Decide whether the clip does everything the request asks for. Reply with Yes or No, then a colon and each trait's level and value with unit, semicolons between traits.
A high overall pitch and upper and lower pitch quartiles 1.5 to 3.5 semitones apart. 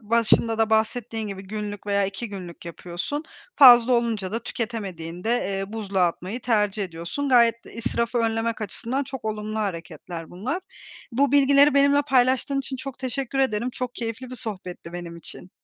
No: high, 225 Hz; average, 4.3 semitones